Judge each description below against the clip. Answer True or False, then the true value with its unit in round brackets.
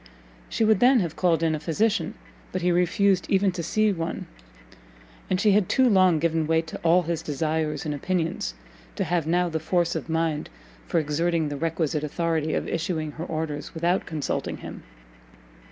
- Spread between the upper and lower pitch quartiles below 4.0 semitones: True (2.5 semitones)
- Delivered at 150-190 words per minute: True (180 wpm)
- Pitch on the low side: False (165 Hz)